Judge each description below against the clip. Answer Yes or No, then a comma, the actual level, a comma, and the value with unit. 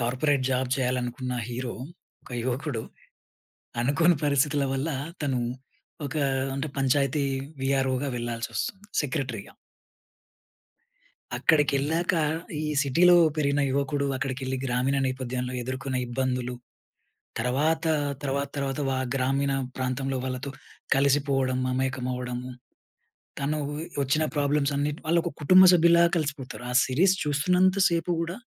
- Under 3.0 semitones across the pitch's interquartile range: Yes, narrow, 2.5 semitones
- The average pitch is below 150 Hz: Yes, low, 135 Hz